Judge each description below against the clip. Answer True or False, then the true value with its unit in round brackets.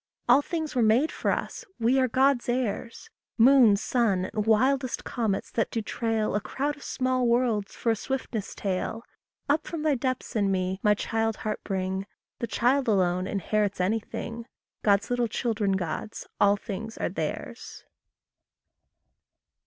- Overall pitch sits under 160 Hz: False (225 Hz)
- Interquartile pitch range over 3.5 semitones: True (4.0 semitones)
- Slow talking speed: False (155 wpm)